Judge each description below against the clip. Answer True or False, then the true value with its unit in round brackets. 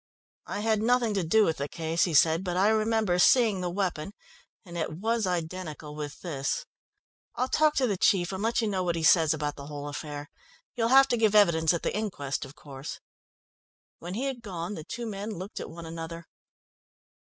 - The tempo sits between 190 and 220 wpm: True (205 wpm)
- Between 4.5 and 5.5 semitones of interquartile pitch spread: True (5.2 semitones)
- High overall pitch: False (180 Hz)